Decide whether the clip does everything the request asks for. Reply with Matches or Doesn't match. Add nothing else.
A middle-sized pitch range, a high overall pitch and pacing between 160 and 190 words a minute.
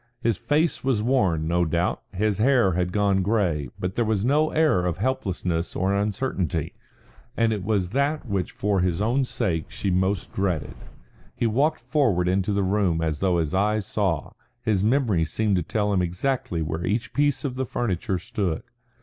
Doesn't match